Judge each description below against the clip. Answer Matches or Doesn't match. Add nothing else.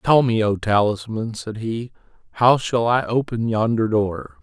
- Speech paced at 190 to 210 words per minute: Doesn't match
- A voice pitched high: Doesn't match